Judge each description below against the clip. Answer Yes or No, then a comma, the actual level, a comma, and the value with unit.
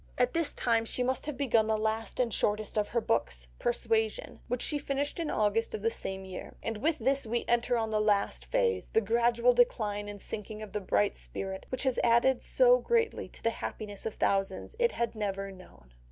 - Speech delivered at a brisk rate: Yes, fast, 210 wpm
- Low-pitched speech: No, high, 225 Hz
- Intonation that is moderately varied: Yes, average, 3.2 semitones